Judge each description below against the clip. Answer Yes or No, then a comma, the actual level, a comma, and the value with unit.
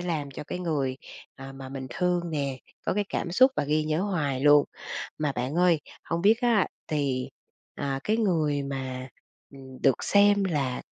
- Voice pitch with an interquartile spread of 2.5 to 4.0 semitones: No, average, 4.7 semitones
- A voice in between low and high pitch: Yes, medium, 150 Hz